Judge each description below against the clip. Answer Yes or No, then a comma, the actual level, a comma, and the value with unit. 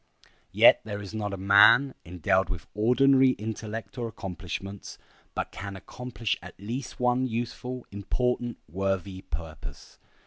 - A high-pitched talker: No, low, 105 Hz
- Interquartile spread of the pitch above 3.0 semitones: Yes, average, 4.3 semitones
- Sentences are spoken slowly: Yes, slow, 130 wpm